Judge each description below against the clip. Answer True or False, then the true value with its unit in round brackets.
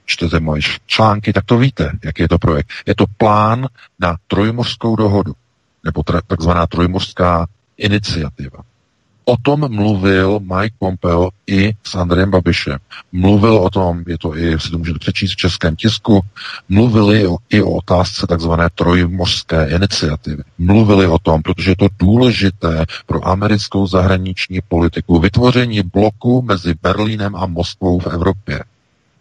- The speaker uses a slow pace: False (140 wpm)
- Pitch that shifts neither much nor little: True (3.3 semitones)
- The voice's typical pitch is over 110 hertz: False (95 Hz)